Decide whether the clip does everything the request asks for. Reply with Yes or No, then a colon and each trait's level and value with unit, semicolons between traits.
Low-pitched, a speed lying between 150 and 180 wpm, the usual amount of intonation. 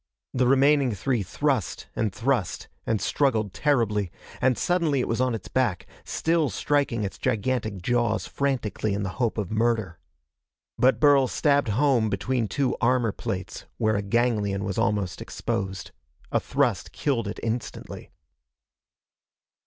No: low, 115 Hz; average, 140 wpm; average, 4.3 semitones